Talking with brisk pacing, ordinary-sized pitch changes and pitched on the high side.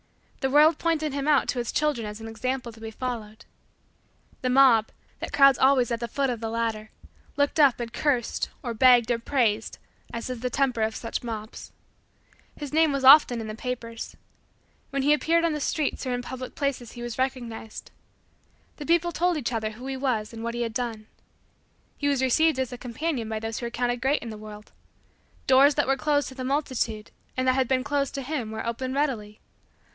Yes: fast, 210 wpm; average, 3.4 semitones; very high, 255 Hz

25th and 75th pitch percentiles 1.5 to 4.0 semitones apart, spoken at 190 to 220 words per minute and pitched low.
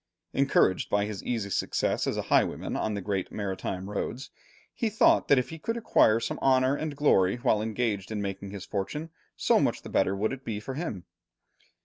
No: average, 5.3 semitones; average, 200 wpm; low, 110 Hz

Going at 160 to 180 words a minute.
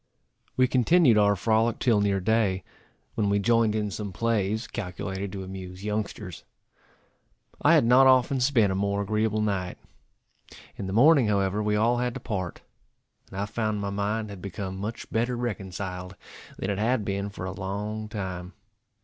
Yes: average, 165 wpm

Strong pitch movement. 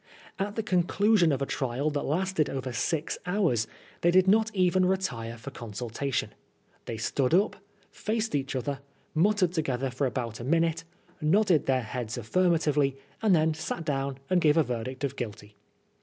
Yes: wide, 6.1 semitones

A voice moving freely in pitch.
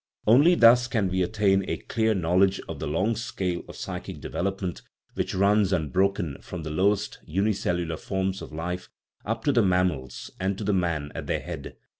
No: average, 3.3 semitones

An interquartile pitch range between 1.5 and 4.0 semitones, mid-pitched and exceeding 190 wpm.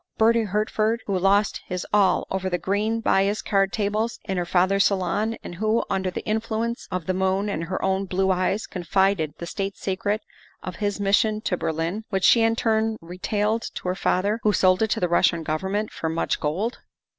No: average, 2.8 semitones; high, 195 Hz; average, 200 wpm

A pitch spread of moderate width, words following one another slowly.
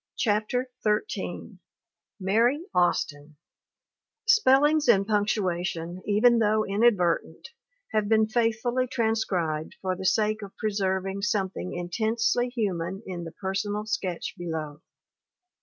Yes: average, 3.6 semitones; slow, 110 wpm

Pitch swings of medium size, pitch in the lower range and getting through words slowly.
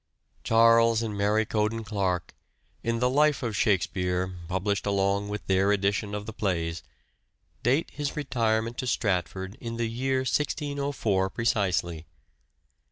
Yes: average, 3.2 semitones; low, 105 Hz; slow, 130 wpm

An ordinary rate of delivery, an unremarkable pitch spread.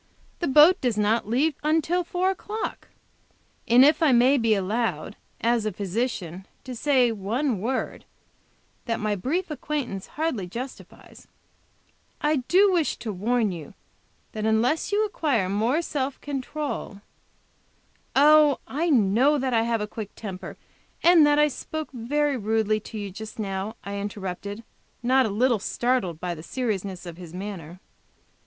No: average, 150 wpm; wide, 6.2 semitones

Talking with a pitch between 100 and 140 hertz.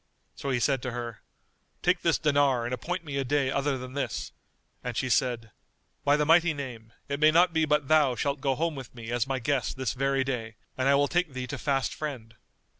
Yes: low, 135 Hz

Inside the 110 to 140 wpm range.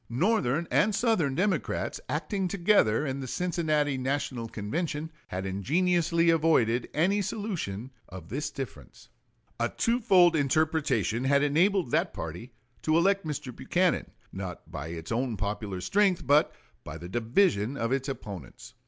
Yes: slow, 135 wpm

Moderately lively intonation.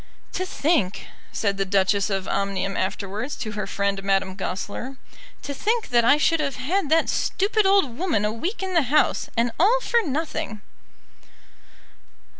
No: wide, 8.8 semitones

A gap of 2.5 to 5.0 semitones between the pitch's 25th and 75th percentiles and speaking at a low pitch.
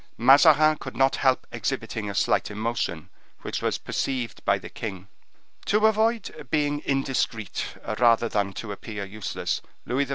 No: wide, 5.4 semitones; low, 125 Hz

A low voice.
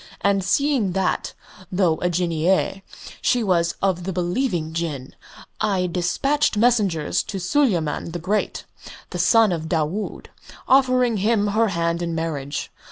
No: medium, 185 Hz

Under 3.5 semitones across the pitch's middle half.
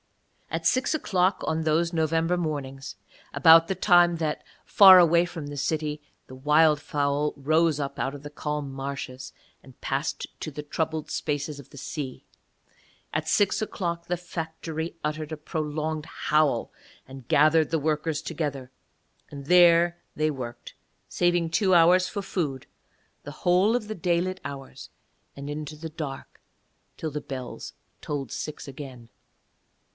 Yes: average, 2.9 semitones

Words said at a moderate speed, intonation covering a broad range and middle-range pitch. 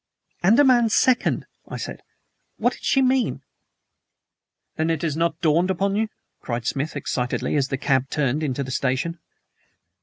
Yes: average, 150 wpm; wide, 6.6 semitones; medium, 160 Hz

